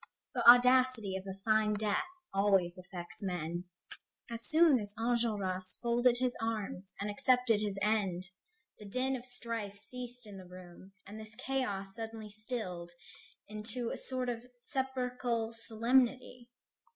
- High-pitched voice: Yes, high, 220 Hz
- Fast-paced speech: No, average, 140 wpm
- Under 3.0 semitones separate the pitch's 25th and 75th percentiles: No, average, 4.0 semitones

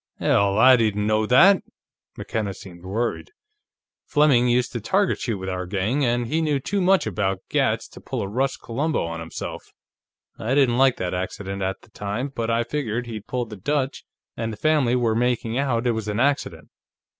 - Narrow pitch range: No, average, 4.6 semitones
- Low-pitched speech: Yes, low, 115 Hz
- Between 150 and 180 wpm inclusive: No, average, 190 wpm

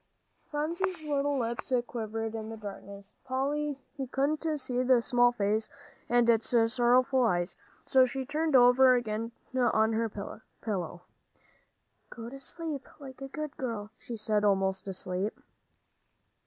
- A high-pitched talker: Yes, high, 240 Hz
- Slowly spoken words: Yes, slow, 130 wpm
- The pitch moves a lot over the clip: No, average, 3.8 semitones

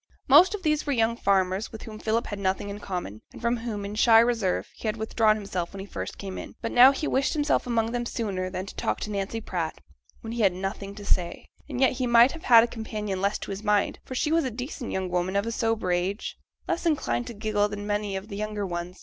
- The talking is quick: Yes, fast, 260 wpm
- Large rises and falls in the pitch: No, average, 3.2 semitones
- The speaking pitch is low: No, high, 215 Hz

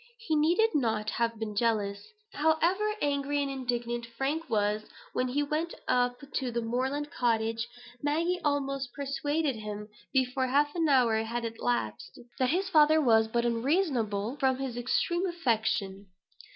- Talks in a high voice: Yes, very high, 260 Hz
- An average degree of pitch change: Yes, average, 4.5 semitones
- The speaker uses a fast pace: No, average, 145 wpm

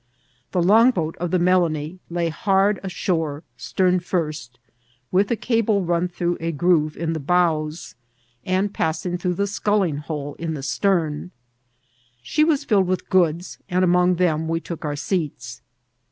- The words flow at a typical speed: Yes, average, 155 wpm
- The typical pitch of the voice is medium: Yes, medium, 175 Hz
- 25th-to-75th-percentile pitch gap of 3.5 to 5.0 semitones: No, average, 2.9 semitones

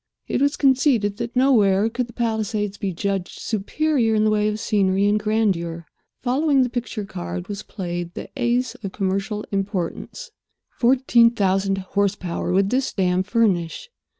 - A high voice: Yes, high, 210 Hz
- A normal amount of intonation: Yes, average, 3.7 semitones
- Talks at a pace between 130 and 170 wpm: Yes, average, 150 wpm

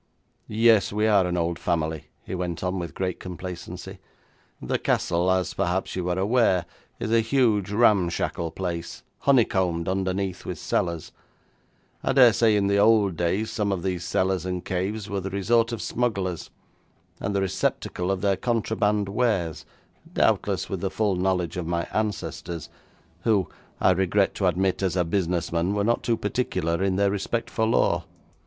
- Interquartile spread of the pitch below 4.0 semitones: Yes, average, 2.9 semitones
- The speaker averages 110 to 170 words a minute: Yes, average, 165 wpm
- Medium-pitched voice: No, very low, 95 Hz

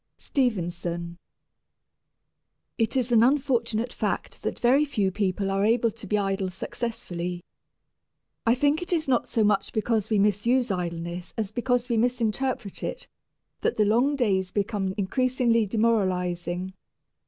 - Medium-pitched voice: No, high, 215 Hz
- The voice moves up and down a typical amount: Yes, average, 4.4 semitones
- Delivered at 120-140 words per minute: Yes, slow, 135 wpm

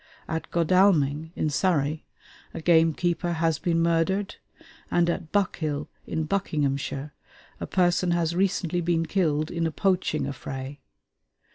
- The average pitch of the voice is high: No, medium, 165 Hz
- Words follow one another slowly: Yes, slow, 125 wpm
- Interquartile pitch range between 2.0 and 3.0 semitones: Yes, narrow, 2.5 semitones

